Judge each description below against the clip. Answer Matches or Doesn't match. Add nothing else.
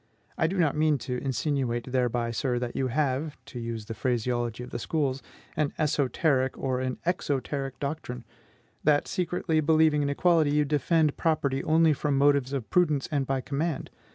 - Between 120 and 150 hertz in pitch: Matches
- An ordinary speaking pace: Matches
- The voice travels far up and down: Doesn't match